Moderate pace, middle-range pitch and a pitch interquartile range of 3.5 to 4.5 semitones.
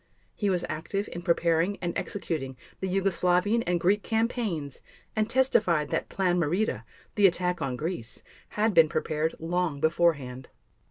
Yes: average, 145 wpm; medium, 175 Hz; average, 3.8 semitones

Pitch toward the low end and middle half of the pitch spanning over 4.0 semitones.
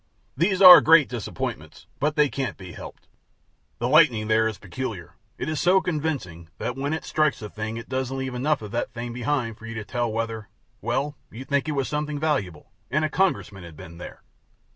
Yes: low, 130 Hz; wide, 5.4 semitones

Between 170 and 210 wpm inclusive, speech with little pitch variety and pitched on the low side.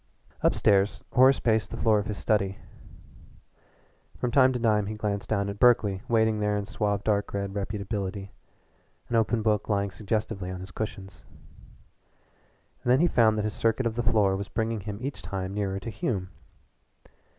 Yes: average, 175 wpm; narrow, 2.2 semitones; low, 105 Hz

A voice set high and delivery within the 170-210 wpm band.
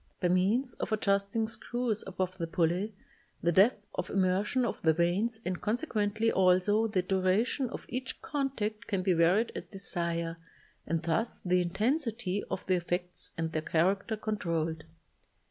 No: high, 195 Hz; average, 155 wpm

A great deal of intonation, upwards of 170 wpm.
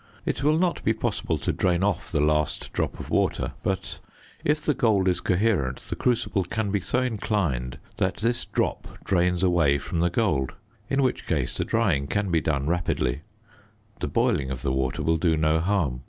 Yes: wide, 5.8 semitones; average, 190 wpm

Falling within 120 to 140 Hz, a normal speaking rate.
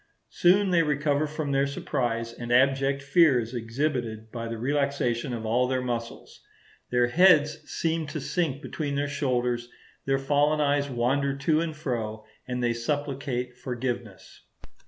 Yes: low, 135 Hz; average, 150 wpm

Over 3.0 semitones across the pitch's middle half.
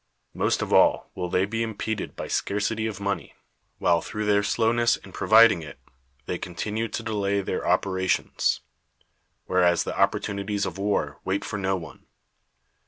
No: average, 2.7 semitones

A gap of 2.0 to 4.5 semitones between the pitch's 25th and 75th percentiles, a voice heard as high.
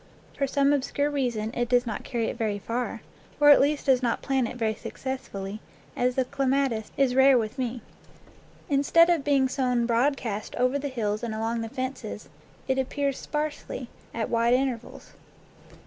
Yes: average, 3.1 semitones; very high, 255 Hz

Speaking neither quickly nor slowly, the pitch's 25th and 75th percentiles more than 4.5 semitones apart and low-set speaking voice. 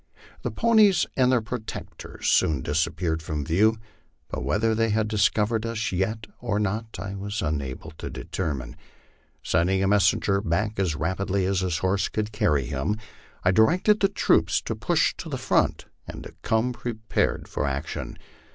Yes: average, 160 wpm; average, 5.1 semitones; low, 100 Hz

